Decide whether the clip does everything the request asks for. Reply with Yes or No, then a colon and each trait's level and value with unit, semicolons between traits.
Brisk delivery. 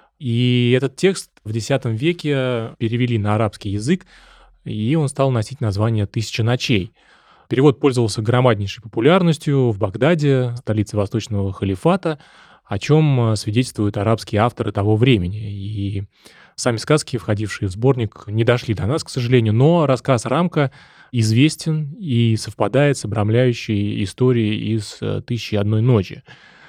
No: average, 130 wpm